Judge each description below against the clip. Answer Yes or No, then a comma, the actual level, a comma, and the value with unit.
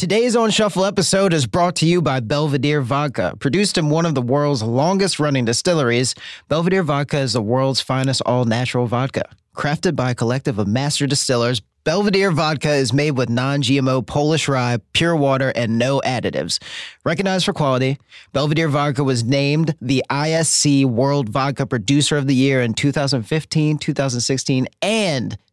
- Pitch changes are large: No, average, 3.3 semitones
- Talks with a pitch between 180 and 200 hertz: No, medium, 140 Hz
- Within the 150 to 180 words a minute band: Yes, average, 160 wpm